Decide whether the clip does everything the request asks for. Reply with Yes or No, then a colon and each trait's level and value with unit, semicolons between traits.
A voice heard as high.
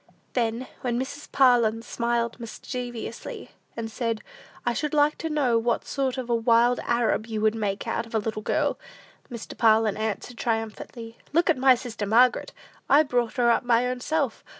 Yes: high, 235 Hz